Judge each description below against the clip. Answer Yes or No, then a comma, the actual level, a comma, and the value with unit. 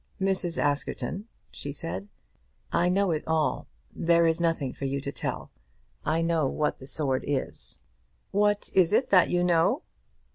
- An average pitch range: Yes, average, 4.0 semitones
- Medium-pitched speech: Yes, medium, 165 Hz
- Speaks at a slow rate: No, average, 155 wpm